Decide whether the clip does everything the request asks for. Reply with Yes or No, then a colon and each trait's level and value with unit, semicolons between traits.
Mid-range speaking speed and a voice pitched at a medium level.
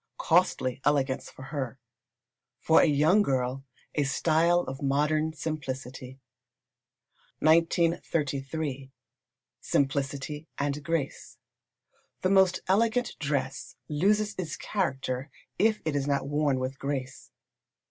No: slow, 105 wpm; medium, 145 Hz